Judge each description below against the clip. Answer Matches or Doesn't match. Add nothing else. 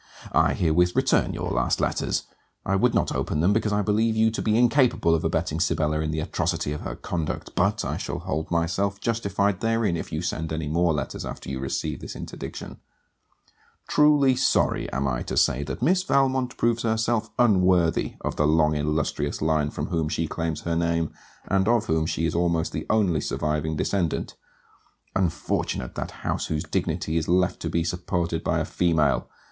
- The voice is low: Matches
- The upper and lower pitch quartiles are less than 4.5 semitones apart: Doesn't match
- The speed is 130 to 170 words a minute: Doesn't match